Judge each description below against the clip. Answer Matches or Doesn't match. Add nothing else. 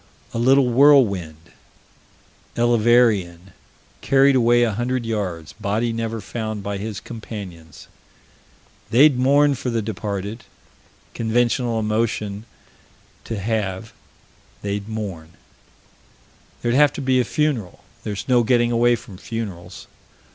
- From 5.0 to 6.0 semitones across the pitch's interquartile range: Doesn't match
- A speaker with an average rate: Doesn't match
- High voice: Doesn't match